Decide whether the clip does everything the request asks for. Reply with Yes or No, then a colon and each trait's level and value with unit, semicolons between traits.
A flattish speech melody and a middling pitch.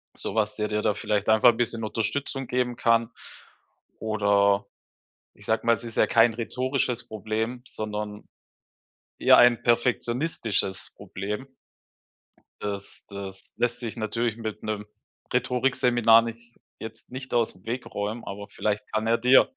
No: narrow, 2.3 semitones; low, 115 Hz